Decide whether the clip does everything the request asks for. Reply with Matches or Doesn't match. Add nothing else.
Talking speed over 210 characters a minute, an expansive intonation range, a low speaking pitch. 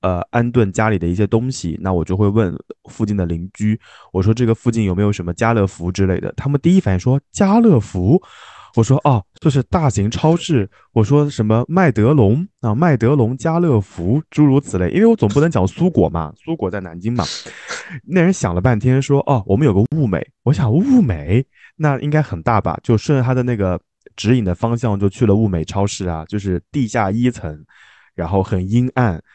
Matches